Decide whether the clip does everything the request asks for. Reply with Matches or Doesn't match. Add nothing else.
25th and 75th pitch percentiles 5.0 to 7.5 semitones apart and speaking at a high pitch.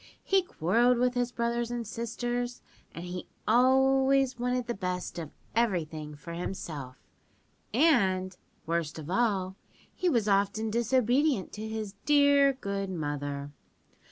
Matches